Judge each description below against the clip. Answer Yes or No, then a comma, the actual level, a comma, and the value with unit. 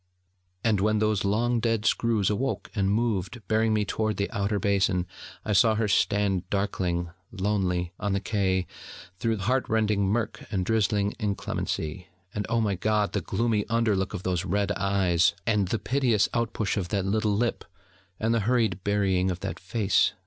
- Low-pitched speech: Yes, low, 105 Hz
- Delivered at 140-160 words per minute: No, average, 175 wpm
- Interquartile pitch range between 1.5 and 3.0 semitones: Yes, narrow, 2.5 semitones